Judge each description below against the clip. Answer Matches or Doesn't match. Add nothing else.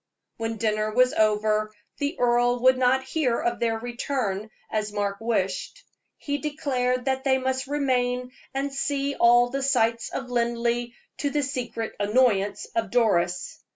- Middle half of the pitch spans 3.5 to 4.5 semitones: Doesn't match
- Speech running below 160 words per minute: Matches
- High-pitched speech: Matches